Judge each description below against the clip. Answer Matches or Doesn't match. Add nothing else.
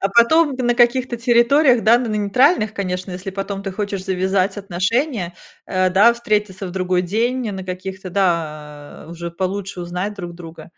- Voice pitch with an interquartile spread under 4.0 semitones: Doesn't match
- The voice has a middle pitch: Doesn't match